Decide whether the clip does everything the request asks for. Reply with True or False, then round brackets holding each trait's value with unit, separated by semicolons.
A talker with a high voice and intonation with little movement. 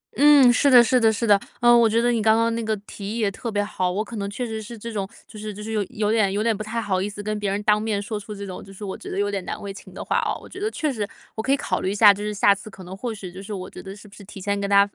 True (210 Hz; 2.3 semitones)